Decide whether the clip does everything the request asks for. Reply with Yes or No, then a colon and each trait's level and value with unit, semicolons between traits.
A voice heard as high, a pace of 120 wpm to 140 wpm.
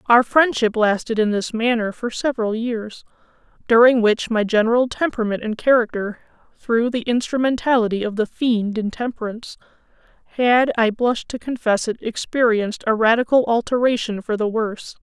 Yes: high, 230 Hz; slow, 135 wpm